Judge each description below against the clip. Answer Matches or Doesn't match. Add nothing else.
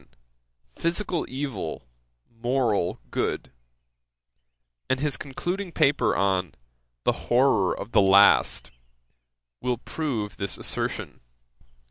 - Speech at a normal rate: Doesn't match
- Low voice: Matches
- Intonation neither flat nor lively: Doesn't match